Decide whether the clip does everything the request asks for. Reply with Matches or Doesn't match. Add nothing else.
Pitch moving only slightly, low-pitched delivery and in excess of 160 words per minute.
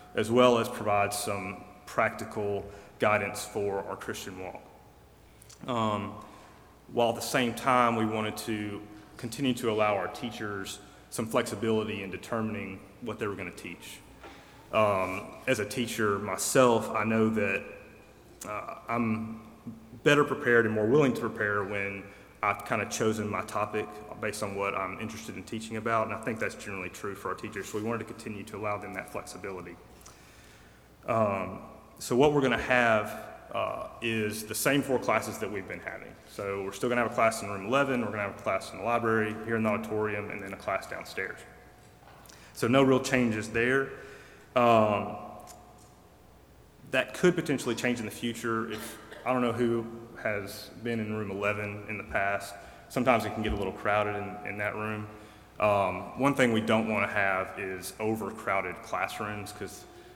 Matches